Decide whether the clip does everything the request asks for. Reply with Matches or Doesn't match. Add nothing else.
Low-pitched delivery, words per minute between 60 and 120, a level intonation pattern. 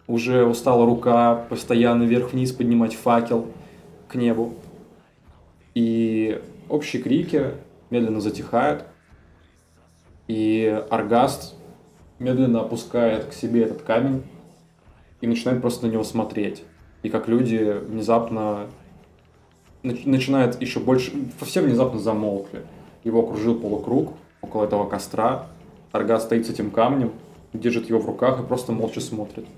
Matches